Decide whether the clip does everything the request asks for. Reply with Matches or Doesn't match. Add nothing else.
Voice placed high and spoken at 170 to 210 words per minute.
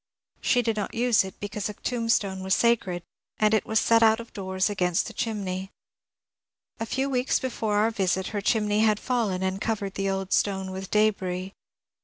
Matches